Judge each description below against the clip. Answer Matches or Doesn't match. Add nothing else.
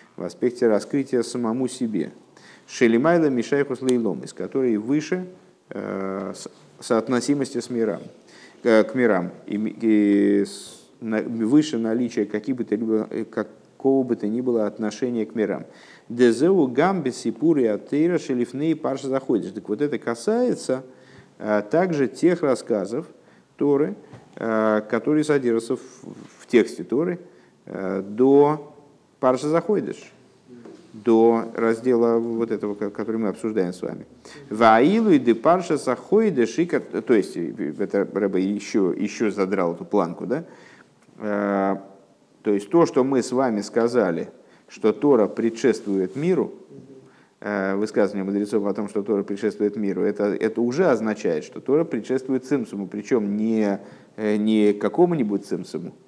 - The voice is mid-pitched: Doesn't match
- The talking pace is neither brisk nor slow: Matches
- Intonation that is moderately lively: Matches